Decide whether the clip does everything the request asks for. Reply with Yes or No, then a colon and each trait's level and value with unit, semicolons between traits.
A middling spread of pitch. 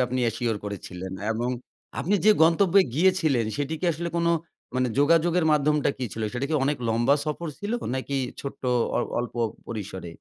No: wide, 6.0 semitones